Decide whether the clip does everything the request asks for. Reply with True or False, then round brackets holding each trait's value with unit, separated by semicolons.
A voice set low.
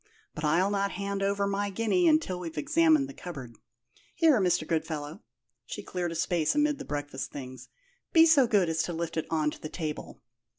False (180 Hz)